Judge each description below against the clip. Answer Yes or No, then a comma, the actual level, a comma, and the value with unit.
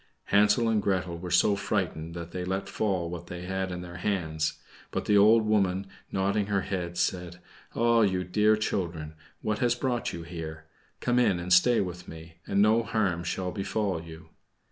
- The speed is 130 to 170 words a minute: No, average, 185 wpm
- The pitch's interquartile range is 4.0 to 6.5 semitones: No, average, 3.3 semitones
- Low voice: Yes, very low, 95 Hz